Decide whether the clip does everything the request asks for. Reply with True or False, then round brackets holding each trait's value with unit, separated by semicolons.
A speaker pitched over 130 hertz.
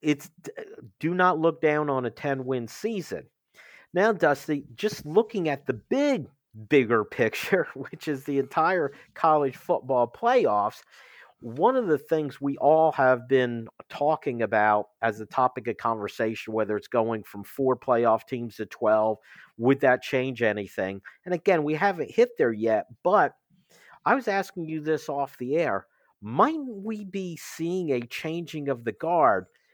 True (140 Hz)